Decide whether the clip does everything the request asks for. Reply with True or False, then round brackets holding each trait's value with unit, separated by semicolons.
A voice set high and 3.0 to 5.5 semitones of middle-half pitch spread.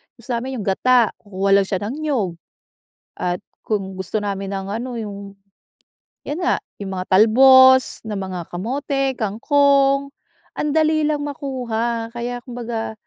True (230 Hz; 5.1 semitones)